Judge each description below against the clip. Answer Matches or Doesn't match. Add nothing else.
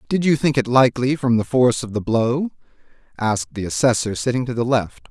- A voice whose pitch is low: Matches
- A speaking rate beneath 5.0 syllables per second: Doesn't match